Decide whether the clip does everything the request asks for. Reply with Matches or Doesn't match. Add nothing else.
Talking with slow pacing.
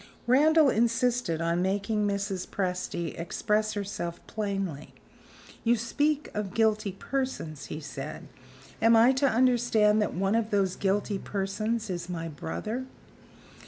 Matches